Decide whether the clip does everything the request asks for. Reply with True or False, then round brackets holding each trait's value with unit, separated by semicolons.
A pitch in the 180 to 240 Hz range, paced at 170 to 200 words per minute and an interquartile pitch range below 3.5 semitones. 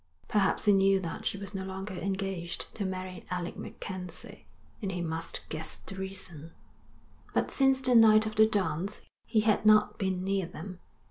True (190 Hz; 175 wpm; 2.6 semitones)